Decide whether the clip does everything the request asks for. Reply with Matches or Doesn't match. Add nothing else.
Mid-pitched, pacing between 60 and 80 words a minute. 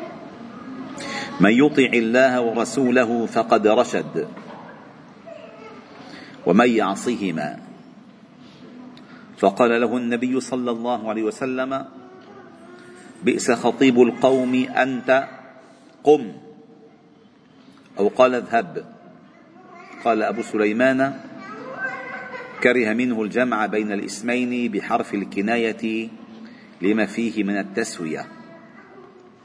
Doesn't match